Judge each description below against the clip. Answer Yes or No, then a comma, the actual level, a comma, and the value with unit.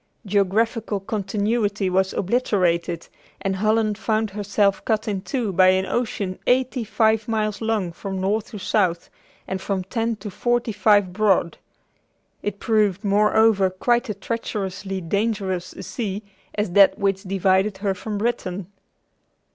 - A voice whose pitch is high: Yes, high, 205 Hz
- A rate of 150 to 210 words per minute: No, average, 140 wpm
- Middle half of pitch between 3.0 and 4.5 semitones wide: No, narrow, 2.4 semitones